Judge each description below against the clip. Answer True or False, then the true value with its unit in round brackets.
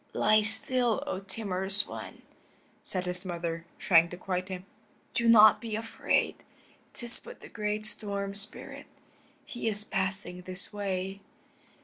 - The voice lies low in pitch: False (200 Hz)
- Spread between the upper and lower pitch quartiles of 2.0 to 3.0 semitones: True (2.7 semitones)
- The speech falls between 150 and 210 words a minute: False (135 wpm)